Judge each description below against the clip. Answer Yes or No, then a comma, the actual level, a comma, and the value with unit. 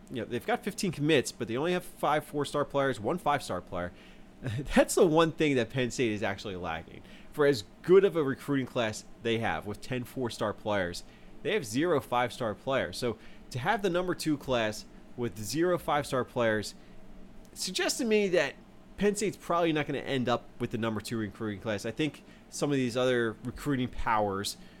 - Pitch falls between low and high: No, low, 125 Hz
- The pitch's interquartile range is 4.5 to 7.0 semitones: Yes, wide, 5.6 semitones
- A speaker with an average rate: Yes, average, 195 wpm